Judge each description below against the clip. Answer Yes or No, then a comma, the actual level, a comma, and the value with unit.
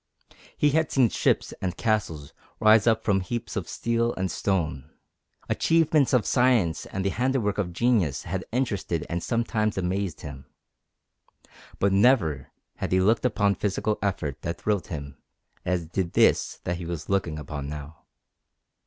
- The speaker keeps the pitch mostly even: No, average, 5.3 semitones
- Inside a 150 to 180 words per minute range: Yes, average, 155 wpm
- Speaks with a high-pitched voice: No, very low, 95 Hz